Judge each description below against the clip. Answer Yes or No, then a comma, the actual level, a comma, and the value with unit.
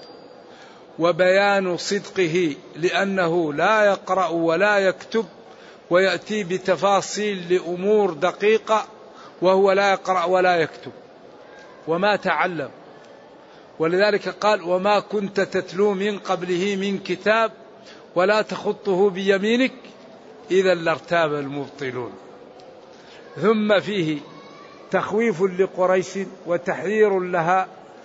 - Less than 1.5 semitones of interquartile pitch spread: No, narrow, 2.6 semitones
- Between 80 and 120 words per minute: Yes, average, 85 wpm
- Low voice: No, high, 190 Hz